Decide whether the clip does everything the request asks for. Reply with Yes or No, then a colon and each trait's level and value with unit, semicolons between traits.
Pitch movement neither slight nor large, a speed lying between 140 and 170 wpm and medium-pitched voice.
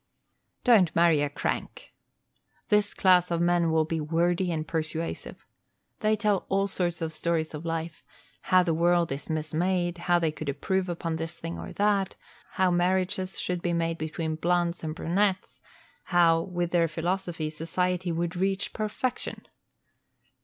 No: narrow, 2.1 semitones; average, 155 wpm; medium, 175 Hz